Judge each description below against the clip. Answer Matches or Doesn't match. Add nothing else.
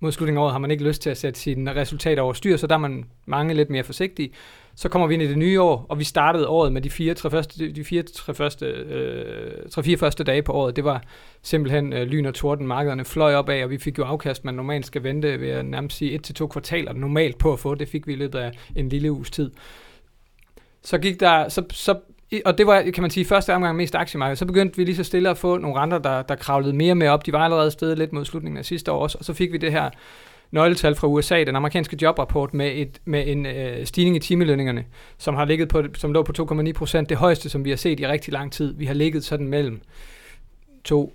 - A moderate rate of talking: Doesn't match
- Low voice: Doesn't match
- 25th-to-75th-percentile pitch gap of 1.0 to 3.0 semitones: Matches